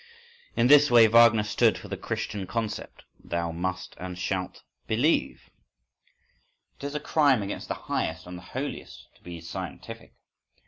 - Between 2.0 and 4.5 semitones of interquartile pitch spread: No, average, 5.3 semitones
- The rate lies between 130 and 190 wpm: Yes, average, 150 wpm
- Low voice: Yes, low, 105 Hz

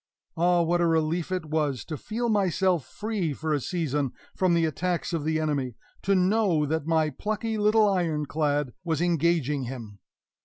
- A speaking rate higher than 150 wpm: Yes, average, 170 wpm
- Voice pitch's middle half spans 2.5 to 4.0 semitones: Yes, average, 3.5 semitones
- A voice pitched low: No, medium, 165 Hz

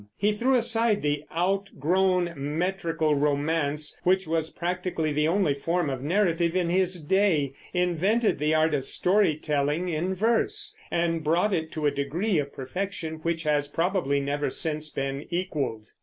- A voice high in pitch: No, medium, 165 Hz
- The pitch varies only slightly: No, average, 4.0 semitones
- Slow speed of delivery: No, average, 155 wpm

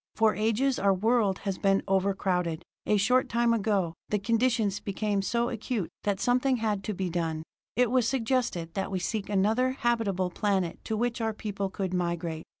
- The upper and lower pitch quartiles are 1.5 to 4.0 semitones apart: Yes, average, 3.5 semitones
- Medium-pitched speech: No, high, 205 Hz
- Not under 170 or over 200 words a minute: Yes, average, 175 wpm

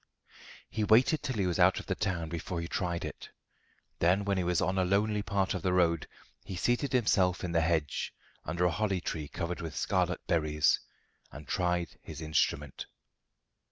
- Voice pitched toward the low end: Yes, very low, 90 Hz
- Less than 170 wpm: No, average, 185 wpm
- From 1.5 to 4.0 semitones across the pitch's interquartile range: Yes, average, 3.0 semitones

